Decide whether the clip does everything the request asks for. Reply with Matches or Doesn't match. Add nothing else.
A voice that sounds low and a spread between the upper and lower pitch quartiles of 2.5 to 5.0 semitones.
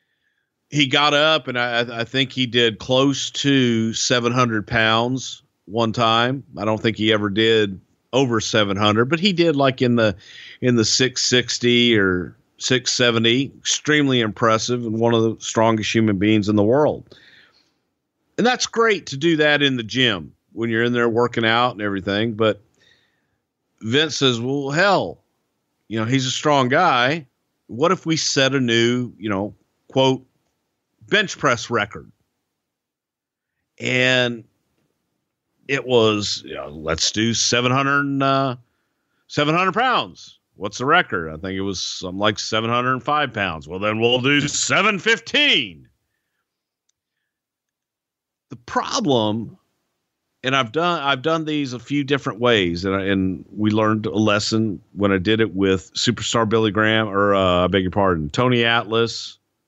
Matches